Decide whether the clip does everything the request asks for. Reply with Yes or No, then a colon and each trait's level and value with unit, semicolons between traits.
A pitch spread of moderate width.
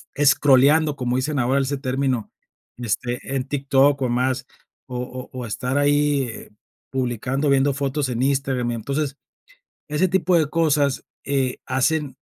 No: narrow, 2.2 semitones